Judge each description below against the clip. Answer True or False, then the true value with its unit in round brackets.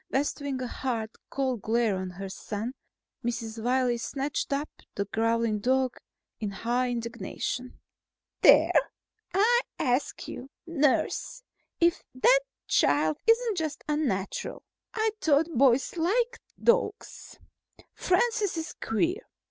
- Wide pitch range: True (6.6 semitones)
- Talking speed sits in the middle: False (115 wpm)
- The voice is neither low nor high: False (260 Hz)